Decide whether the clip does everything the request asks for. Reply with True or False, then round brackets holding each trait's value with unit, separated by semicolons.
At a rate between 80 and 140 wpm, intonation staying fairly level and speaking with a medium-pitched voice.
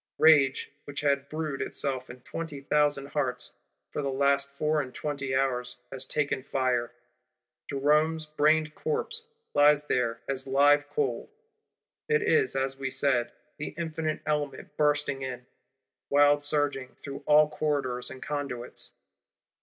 True (135 wpm; 2.1 semitones; 145 Hz)